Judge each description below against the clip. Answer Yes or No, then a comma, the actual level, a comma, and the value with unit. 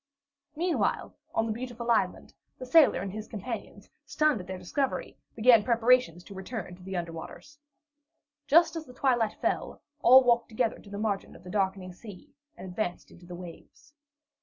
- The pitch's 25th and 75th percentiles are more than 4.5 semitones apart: Yes, average, 5.1 semitones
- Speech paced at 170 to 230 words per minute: Yes, average, 175 wpm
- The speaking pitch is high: Yes, high, 220 Hz